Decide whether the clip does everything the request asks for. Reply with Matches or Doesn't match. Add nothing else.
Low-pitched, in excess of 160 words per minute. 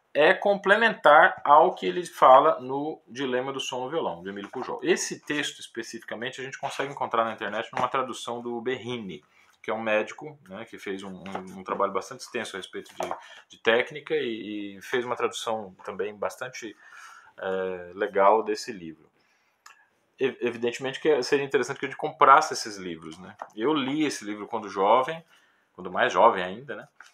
Matches